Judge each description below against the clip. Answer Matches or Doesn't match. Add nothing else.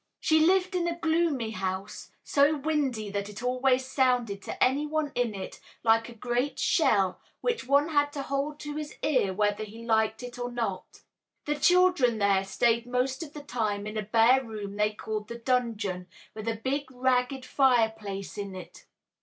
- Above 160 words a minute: Matches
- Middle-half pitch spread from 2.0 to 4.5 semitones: Doesn't match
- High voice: Matches